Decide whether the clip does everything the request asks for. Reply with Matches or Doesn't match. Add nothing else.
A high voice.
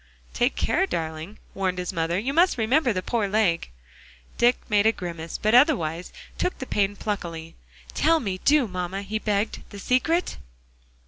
Matches